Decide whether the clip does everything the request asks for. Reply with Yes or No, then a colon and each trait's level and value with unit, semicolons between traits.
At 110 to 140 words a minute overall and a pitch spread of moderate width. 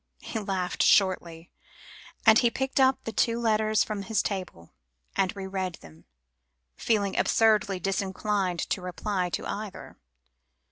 Yes: slow, 135 wpm; average, 3.0 semitones